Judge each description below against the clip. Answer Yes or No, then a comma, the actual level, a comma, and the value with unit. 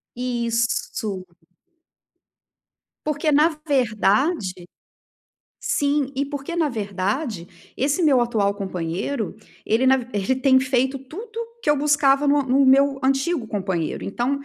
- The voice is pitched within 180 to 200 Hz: No, very high, 260 Hz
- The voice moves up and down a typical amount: Yes, average, 4.9 semitones